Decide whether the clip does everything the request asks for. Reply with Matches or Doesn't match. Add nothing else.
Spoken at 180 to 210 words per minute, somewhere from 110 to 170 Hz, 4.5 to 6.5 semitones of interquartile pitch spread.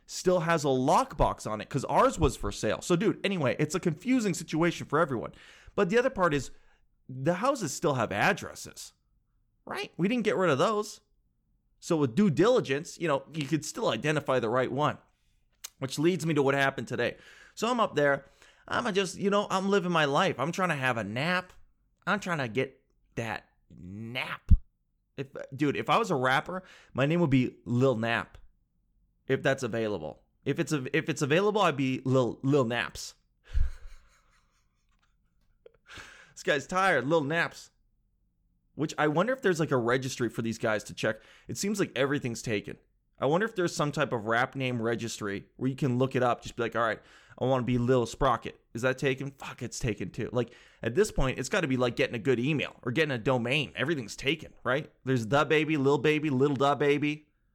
Matches